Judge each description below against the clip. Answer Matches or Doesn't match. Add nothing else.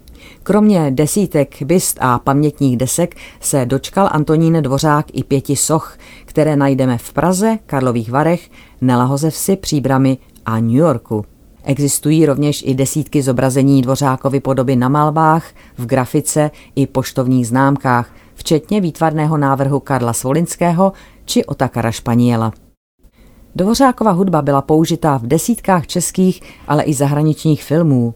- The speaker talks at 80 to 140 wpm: Matches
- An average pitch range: Matches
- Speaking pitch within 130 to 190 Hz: Matches